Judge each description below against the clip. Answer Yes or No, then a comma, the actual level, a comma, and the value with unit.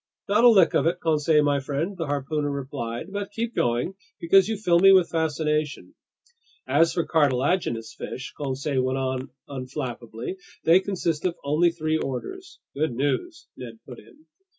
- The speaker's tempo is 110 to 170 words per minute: Yes, average, 160 wpm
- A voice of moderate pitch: Yes, medium, 155 Hz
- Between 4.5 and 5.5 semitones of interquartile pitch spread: Yes, average, 5.2 semitones